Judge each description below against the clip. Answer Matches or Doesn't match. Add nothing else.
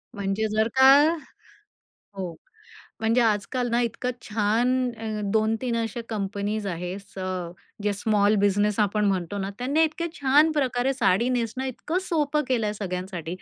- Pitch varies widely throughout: Doesn't match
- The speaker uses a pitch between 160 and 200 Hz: Doesn't match